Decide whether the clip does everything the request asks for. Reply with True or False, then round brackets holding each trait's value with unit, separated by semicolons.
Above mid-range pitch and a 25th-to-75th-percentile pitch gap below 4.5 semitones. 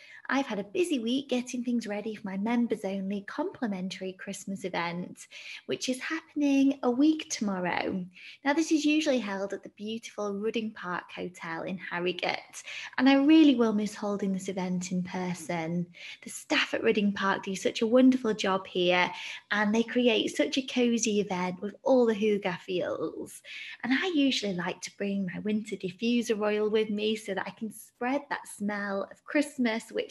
False (215 Hz; 4.8 semitones)